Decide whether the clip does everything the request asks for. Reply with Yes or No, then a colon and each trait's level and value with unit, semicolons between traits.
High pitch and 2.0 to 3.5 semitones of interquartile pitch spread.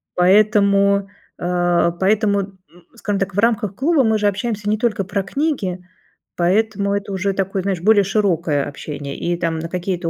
Yes: high, 195 Hz; average, 2.8 semitones